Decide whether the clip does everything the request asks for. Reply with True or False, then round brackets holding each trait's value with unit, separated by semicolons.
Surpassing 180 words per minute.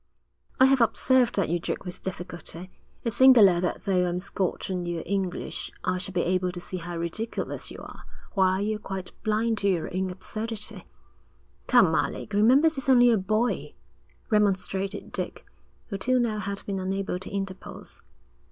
False (170 wpm)